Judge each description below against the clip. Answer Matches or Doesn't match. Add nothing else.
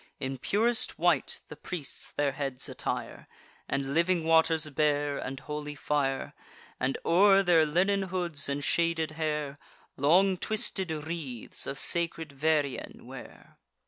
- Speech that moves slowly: Matches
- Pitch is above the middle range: Doesn't match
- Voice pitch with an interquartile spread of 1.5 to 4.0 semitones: Matches